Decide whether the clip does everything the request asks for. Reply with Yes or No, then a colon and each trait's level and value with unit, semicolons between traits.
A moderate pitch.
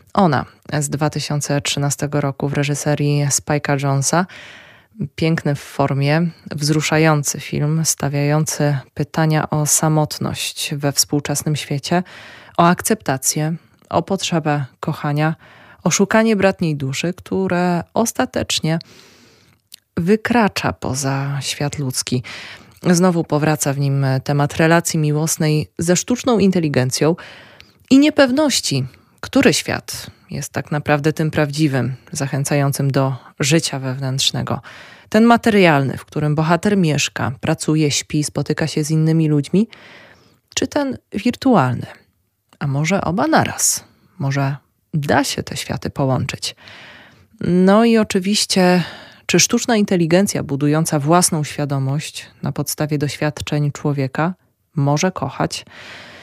Yes: medium, 150 Hz